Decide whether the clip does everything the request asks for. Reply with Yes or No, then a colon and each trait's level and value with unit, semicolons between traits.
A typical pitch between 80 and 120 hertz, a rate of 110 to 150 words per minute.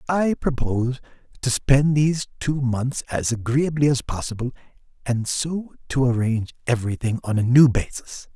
No: low, 130 Hz; average, 145 wpm